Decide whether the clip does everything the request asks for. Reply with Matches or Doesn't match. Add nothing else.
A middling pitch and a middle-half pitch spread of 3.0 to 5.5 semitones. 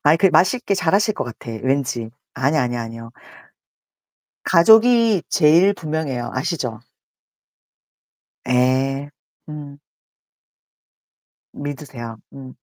Matches